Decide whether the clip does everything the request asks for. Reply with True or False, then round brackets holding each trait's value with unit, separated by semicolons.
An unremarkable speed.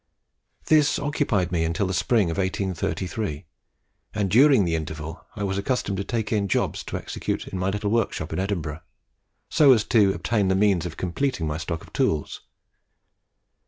True (170 wpm)